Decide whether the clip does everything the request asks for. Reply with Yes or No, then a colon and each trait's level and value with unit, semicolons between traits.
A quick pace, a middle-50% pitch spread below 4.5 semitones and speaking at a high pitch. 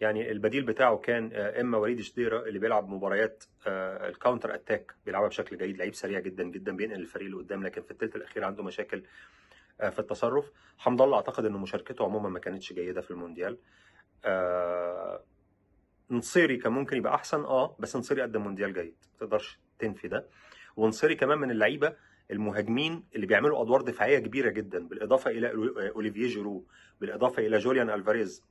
No: fast, 160 wpm; average, 3.6 semitones; low, 110 Hz